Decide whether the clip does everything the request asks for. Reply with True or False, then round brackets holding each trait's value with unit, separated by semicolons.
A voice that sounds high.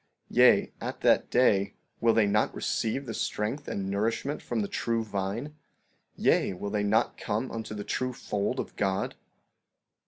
False (110 Hz)